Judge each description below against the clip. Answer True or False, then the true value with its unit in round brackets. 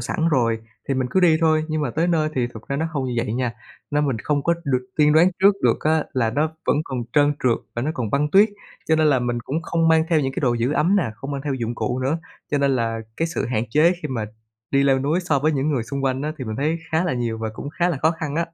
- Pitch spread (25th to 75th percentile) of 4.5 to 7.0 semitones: False (4.0 semitones)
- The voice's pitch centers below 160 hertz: True (140 Hz)